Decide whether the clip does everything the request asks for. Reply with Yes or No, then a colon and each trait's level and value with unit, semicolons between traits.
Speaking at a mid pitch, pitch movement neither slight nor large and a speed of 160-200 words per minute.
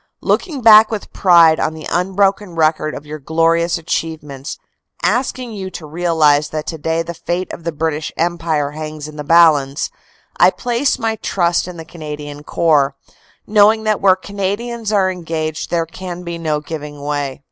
Yes: medium, 165 Hz; average, 3.7 semitones; average, 165 wpm